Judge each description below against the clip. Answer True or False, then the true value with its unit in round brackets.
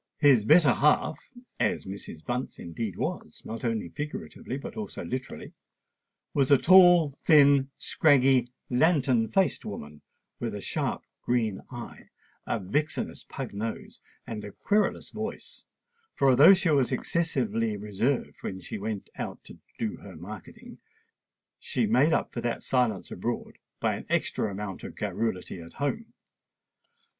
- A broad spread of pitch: True (5.9 semitones)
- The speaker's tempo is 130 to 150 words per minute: True (135 wpm)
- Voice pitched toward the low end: True (125 Hz)